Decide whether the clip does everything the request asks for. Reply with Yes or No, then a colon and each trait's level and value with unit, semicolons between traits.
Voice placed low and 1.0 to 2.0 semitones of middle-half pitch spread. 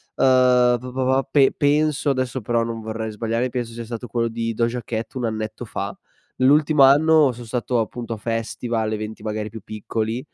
No: low, 120 Hz; narrow, 2.5 semitones